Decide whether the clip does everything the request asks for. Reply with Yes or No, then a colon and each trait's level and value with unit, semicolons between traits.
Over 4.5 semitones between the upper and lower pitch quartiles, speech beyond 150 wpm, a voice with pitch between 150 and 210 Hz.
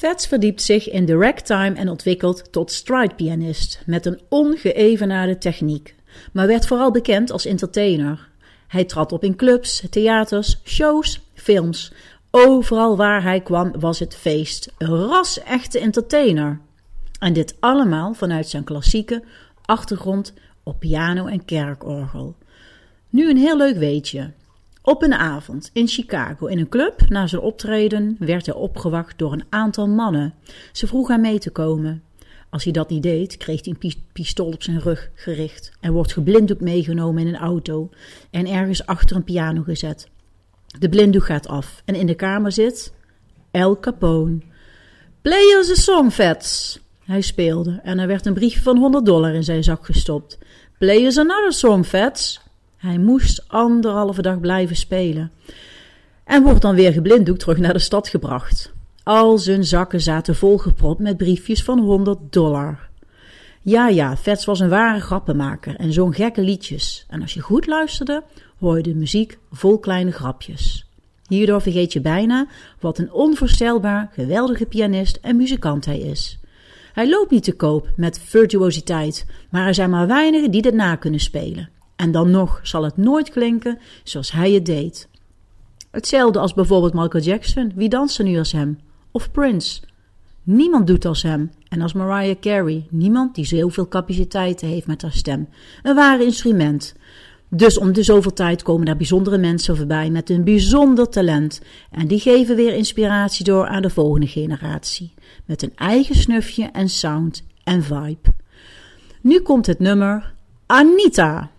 Yes: wide, 5.4 semitones; average, 160 wpm; medium, 185 Hz